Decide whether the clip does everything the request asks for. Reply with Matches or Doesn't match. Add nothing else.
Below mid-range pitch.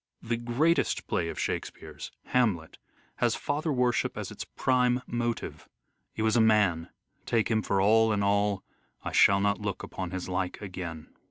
Matches